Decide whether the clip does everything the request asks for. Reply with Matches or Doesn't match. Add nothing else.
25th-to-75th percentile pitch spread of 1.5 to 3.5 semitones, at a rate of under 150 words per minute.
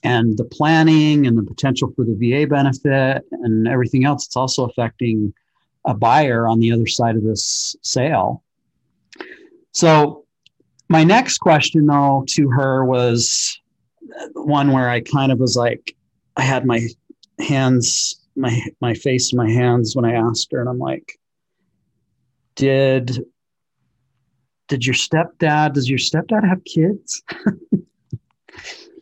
Doesn't match